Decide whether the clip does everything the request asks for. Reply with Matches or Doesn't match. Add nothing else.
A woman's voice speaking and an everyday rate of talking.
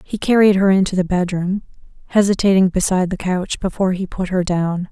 Matches